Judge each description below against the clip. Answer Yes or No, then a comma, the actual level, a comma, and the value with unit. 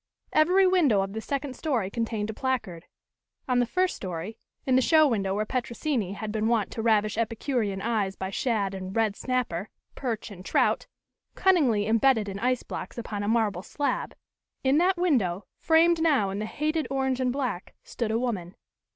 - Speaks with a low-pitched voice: No, high, 230 Hz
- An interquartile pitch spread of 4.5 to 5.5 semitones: Yes, average, 4.9 semitones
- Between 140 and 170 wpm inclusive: No, average, 180 wpm